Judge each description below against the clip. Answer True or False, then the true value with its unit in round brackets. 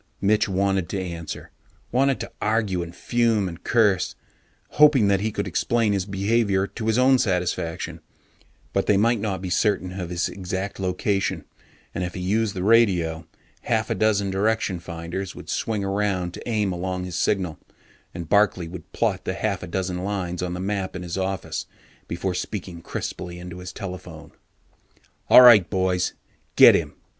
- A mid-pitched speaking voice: False (95 Hz)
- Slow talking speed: False (170 wpm)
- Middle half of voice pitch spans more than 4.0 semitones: False (2.7 semitones)